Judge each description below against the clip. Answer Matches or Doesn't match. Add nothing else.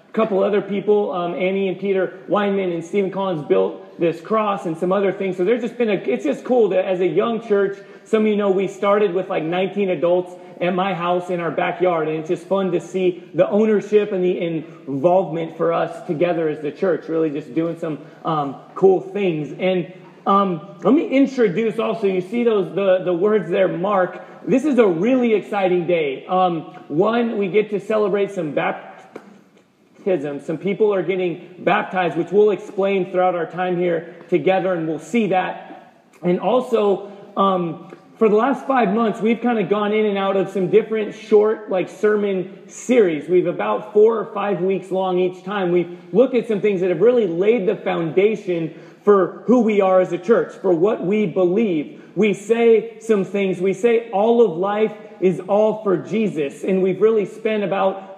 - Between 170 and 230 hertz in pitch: Matches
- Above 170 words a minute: Matches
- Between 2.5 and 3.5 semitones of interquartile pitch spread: Matches